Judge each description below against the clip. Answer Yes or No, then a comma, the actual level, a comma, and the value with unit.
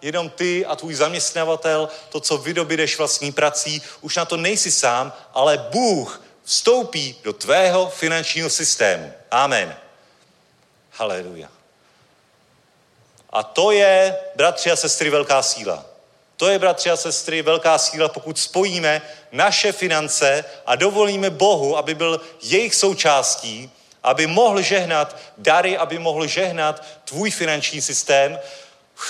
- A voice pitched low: No, medium, 160 Hz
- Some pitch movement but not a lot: Yes, average, 3.4 semitones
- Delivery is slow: No, average, 125 wpm